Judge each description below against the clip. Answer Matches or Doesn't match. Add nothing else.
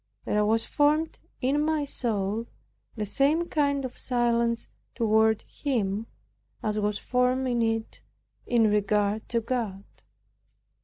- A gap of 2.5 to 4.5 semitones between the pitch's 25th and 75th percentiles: Matches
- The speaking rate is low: Matches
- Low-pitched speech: Doesn't match